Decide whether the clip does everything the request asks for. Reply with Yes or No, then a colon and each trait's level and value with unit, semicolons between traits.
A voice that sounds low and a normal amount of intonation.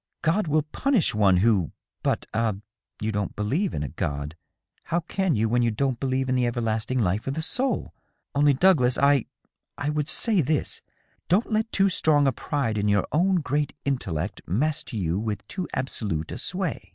No: low, 130 Hz; wide, 6.6 semitones